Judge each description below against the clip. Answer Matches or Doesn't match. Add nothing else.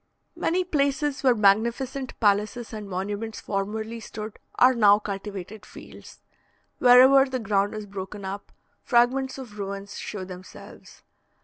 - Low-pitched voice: Doesn't match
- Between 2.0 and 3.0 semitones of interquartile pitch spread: Doesn't match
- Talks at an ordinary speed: Doesn't match